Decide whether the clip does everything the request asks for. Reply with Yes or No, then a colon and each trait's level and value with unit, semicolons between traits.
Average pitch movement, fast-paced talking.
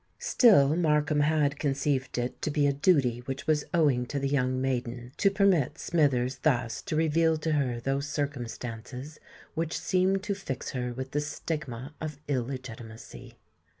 No: average, 3.5 semitones; average, 155 wpm